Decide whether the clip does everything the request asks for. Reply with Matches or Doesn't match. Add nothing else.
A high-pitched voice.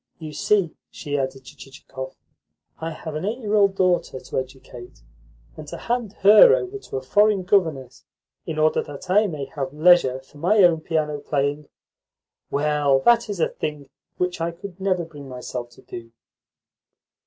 Doesn't match